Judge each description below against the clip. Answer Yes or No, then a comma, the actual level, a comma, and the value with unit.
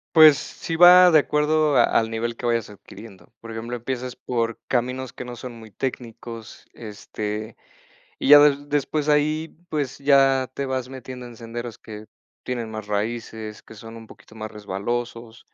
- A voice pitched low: Yes, low, 120 Hz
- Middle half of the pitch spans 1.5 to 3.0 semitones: No, average, 3.6 semitones